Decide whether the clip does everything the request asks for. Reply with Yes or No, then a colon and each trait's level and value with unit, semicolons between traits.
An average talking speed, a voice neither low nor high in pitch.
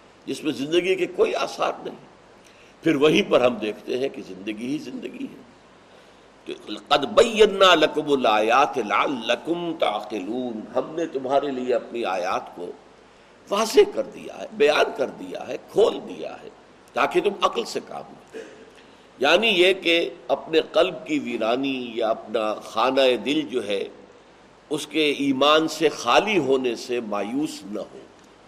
Yes: average, 150 wpm; medium, 155 Hz